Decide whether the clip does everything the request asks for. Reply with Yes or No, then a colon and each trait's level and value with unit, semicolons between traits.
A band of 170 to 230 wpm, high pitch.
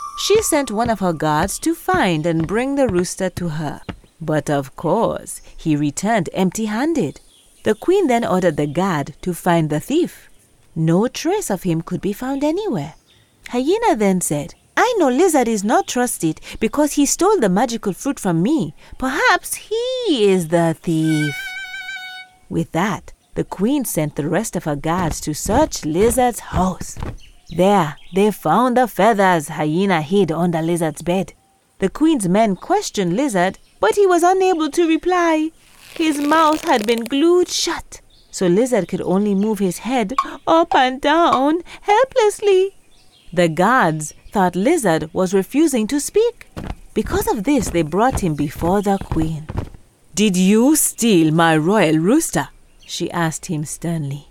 No: average, 155 wpm; high, 205 Hz